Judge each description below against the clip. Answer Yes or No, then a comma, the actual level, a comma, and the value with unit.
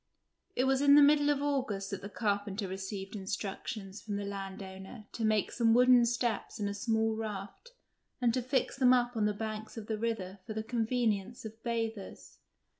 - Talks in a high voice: Yes, high, 220 Hz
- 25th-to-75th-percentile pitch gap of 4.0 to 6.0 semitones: No, average, 3.2 semitones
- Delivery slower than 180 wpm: No, average, 190 wpm